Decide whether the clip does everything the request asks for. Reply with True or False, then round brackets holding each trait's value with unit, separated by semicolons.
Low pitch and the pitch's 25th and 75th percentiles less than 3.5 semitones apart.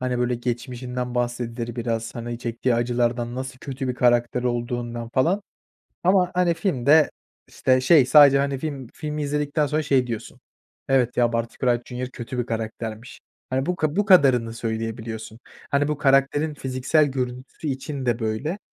True (125 Hz; 3.0 semitones)